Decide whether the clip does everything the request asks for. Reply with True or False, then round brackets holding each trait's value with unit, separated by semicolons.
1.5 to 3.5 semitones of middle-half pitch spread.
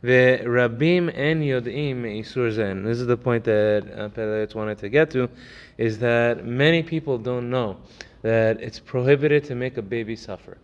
True (2.5 semitones)